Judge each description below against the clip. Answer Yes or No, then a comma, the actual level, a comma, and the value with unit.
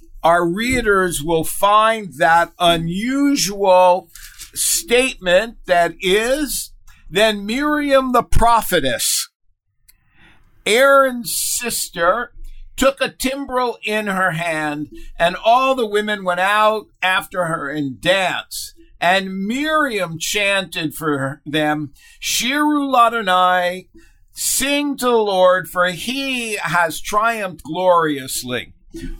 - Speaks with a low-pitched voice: No, high, 190 Hz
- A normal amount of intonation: No, wide, 6.4 semitones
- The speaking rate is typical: No, slow, 100 wpm